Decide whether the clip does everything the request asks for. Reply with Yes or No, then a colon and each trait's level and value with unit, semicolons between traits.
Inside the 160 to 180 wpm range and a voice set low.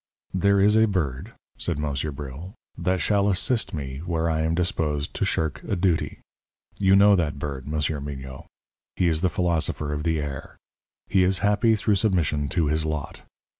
Yes: average, 175 wpm; very low, 80 Hz